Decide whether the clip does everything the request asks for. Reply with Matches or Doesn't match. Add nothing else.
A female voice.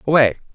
Doesn't match